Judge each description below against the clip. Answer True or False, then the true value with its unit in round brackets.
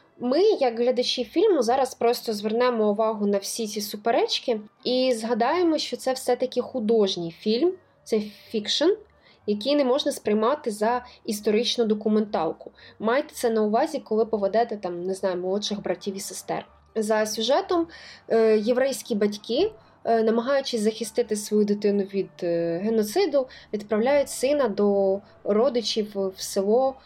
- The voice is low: False (225 Hz)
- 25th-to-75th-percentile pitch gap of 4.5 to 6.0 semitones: False (3.4 semitones)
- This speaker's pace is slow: False (125 wpm)